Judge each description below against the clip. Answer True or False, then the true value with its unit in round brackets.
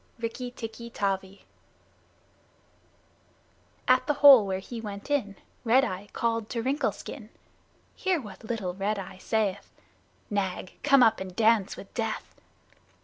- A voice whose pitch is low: False (220 Hz)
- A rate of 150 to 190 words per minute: False (135 wpm)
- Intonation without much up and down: False (3.8 semitones)